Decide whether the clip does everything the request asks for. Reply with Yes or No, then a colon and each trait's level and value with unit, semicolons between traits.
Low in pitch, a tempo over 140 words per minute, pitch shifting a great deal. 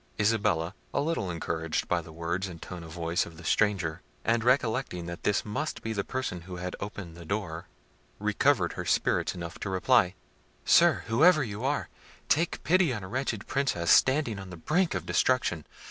Yes: low, 100 Hz; average, 185 wpm; wide, 6.6 semitones